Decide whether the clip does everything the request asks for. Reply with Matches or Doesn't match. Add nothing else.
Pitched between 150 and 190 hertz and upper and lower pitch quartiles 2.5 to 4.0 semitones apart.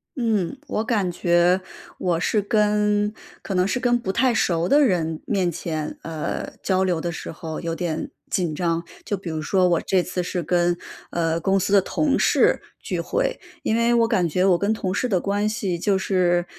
Matches